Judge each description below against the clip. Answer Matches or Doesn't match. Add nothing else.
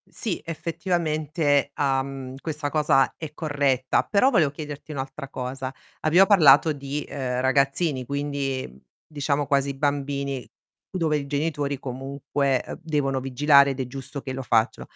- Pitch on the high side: Doesn't match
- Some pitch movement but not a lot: Doesn't match